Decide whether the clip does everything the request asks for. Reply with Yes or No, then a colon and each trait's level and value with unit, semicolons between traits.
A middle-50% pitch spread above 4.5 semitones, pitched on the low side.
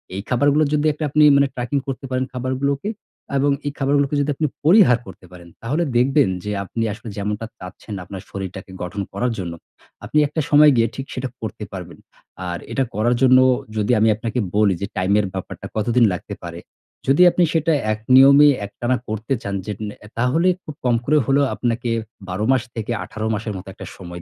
Yes: average, 5.2 semitones; low, 120 Hz